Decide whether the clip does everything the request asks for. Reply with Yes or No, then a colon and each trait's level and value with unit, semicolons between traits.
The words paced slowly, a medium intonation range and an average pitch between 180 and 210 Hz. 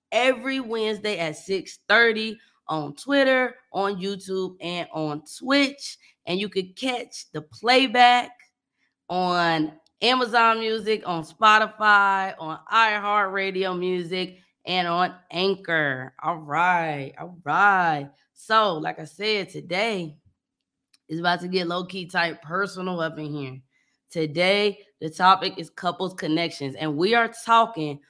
Yes: slow, 120 wpm; average, 4.8 semitones; medium, 185 Hz